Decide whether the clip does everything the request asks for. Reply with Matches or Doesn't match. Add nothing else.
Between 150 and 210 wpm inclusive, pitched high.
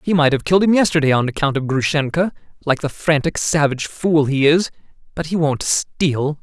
Doesn't match